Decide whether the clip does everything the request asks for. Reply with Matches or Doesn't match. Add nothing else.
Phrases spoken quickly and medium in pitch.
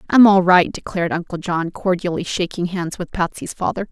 Doesn't match